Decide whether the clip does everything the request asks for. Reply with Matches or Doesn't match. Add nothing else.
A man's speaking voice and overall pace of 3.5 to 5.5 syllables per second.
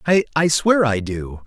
Matches